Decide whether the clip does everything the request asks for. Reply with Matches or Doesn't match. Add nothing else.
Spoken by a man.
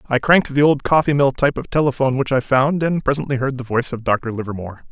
Matches